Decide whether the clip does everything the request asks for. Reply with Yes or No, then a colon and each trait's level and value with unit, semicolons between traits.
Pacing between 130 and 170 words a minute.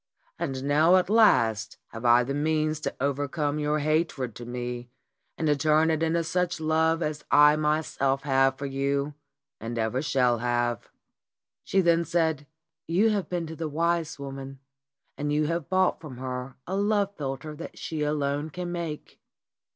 Yes: average, 165 wpm